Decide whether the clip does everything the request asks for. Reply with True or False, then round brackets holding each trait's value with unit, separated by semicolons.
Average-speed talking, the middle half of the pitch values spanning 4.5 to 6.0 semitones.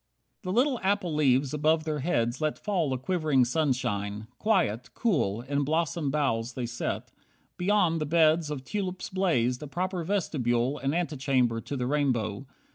True (160 wpm; 5.5 semitones)